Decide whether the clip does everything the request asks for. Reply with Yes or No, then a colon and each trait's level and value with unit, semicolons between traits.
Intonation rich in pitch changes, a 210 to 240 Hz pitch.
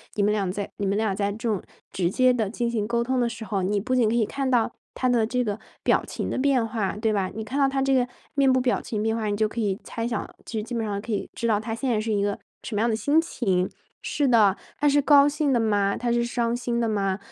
No: average, 3.2 semitones; high, 225 Hz